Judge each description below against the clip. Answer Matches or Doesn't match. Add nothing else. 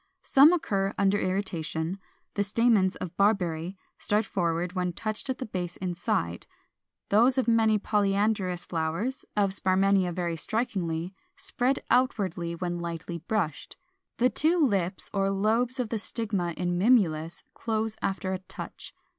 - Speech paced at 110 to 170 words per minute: Matches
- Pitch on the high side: Matches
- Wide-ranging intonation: Doesn't match